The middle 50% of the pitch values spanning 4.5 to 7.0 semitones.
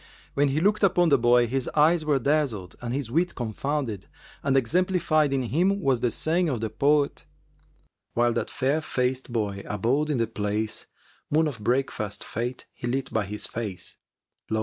Yes: average, 4.8 semitones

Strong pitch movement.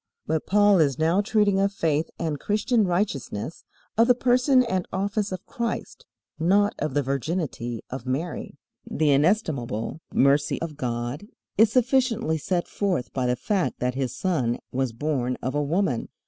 Yes: wide, 7.2 semitones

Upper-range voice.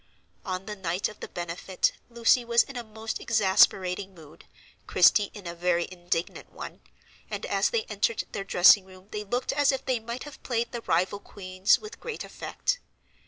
Yes: high, 205 Hz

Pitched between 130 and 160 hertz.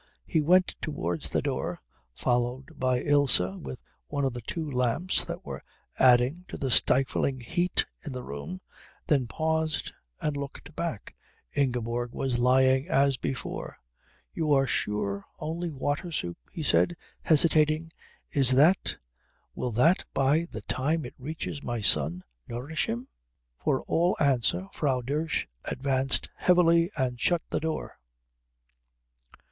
Yes: low, 135 Hz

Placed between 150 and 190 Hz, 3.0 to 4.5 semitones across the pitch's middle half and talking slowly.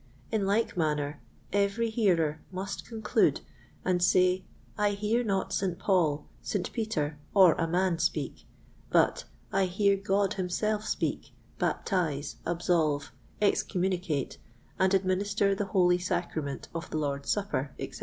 Yes: medium, 185 Hz; average, 3.6 semitones; slow, 130 wpm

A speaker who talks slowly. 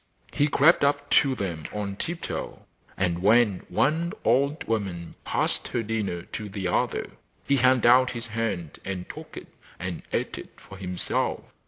No: average, 160 wpm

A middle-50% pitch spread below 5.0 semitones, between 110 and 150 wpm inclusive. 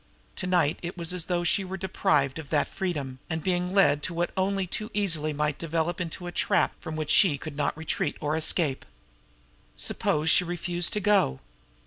No: average, 3.2 semitones; average, 190 wpm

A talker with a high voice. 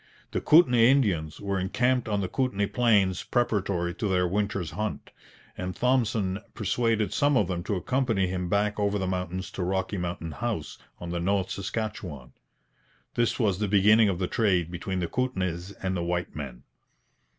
No: low, 100 Hz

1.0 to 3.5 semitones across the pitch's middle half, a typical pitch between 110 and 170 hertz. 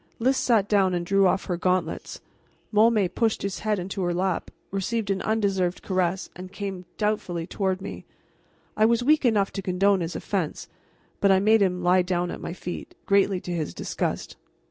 No: narrow, 2.5 semitones; high, 195 Hz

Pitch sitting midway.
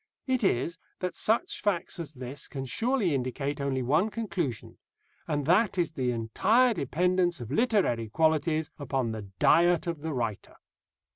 Yes: medium, 155 Hz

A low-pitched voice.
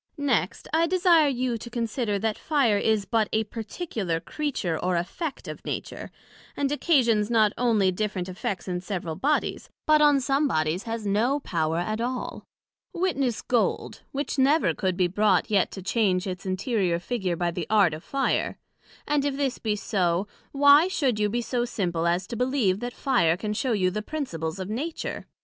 No: high, 220 Hz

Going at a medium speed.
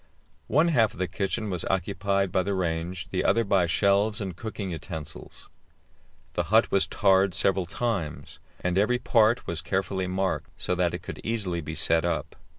Yes: average, 175 wpm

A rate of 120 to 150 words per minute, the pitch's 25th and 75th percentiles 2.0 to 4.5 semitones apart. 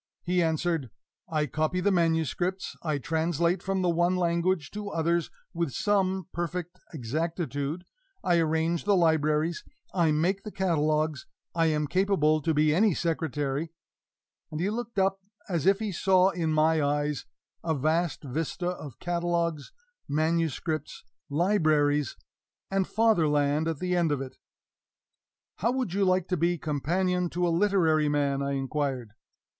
Yes: average, 145 wpm; average, 3.1 semitones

